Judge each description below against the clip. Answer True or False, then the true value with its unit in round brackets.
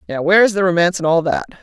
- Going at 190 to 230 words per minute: False (295 wpm)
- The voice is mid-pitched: True (175 Hz)